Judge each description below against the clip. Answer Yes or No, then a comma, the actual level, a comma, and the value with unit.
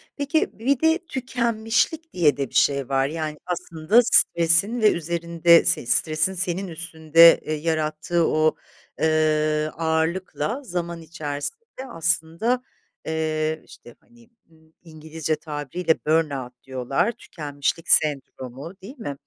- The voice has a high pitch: No, medium, 160 Hz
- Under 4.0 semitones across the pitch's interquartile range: Yes, average, 3.3 semitones